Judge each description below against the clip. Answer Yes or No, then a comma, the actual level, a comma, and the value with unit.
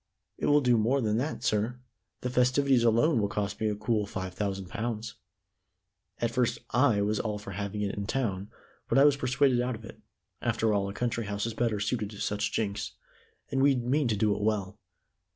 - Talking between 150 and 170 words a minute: No, fast, 205 wpm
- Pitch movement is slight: No, average, 3.4 semitones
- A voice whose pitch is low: Yes, low, 110 Hz